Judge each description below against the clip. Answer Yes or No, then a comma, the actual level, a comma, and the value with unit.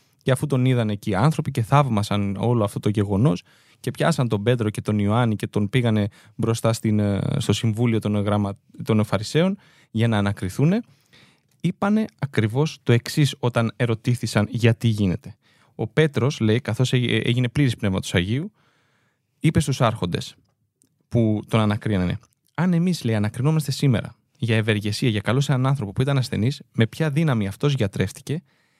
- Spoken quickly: No, average, 155 wpm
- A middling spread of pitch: Yes, average, 4.8 semitones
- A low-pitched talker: Yes, low, 120 Hz